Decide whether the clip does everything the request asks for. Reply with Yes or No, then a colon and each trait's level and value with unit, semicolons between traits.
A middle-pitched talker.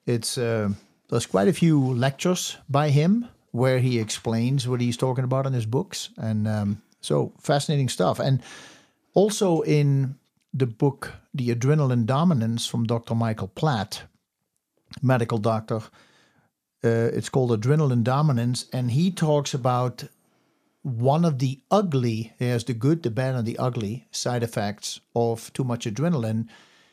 No: low, 125 Hz